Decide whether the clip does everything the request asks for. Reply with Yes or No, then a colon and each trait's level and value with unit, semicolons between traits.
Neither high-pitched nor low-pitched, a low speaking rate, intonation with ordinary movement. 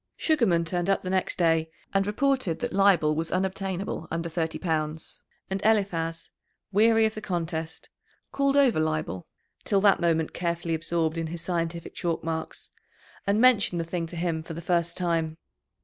No: medium, 170 Hz; average, 165 wpm; average, 3.2 semitones